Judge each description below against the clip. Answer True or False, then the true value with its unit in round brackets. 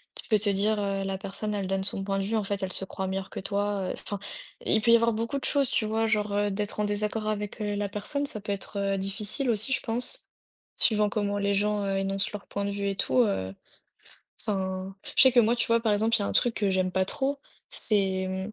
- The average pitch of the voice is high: True (205 Hz)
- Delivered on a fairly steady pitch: True (1.9 semitones)